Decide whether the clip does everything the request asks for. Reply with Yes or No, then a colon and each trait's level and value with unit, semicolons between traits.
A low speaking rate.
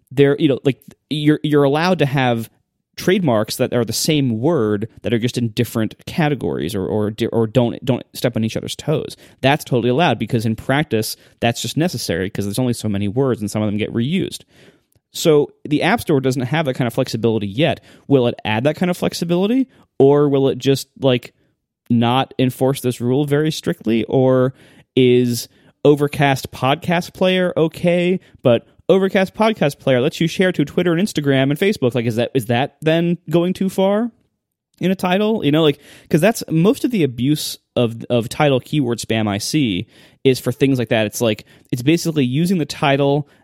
No: average, 195 wpm